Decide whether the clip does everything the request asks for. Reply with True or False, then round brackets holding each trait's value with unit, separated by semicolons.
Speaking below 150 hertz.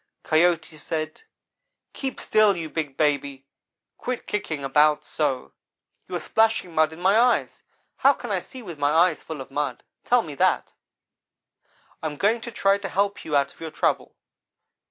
False (160 Hz)